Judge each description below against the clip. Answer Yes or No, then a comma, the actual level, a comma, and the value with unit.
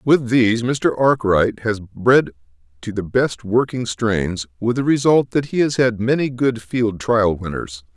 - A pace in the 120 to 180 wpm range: Yes, average, 175 wpm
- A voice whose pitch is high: No, low, 115 Hz